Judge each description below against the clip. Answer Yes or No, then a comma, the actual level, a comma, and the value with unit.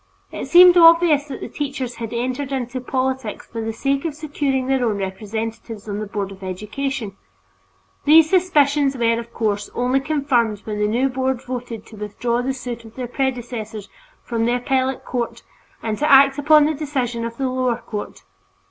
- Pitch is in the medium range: No, very high, 250 Hz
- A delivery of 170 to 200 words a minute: Yes, average, 180 wpm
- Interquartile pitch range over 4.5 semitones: No, average, 3.5 semitones